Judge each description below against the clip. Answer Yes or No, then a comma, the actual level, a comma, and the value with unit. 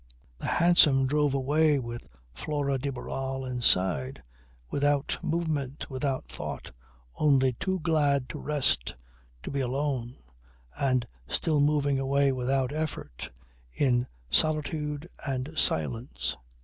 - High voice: No, medium, 140 Hz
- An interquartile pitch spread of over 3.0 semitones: No, narrow, 2.5 semitones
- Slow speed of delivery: Yes, slow, 110 wpm